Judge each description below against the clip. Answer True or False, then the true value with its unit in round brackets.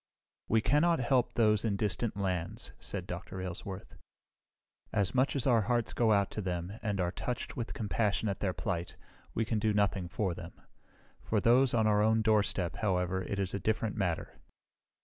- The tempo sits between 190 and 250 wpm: False (180 wpm)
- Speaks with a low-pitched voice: True (105 Hz)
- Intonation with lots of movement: False (3.2 semitones)